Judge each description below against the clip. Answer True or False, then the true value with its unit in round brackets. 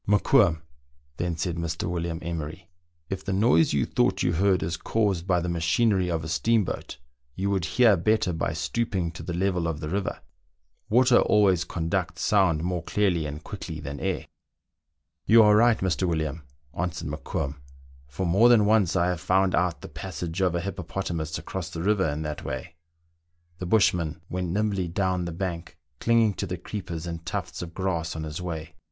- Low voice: True (90 Hz)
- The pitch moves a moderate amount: True (3.1 semitones)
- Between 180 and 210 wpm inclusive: True (190 wpm)